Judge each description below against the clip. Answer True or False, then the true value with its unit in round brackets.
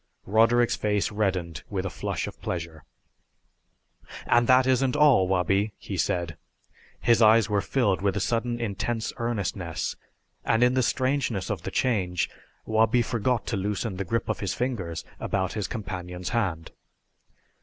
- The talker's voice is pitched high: False (105 Hz)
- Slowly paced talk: False (150 wpm)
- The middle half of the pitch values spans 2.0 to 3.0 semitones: False (4.2 semitones)